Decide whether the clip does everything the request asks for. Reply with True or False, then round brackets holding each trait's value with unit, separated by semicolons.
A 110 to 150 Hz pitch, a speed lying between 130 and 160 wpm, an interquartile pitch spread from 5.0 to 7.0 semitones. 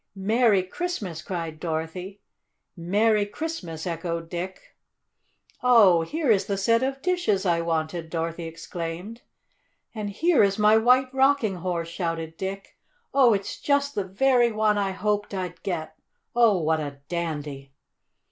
False (190 Hz; 140 wpm; 5.3 semitones)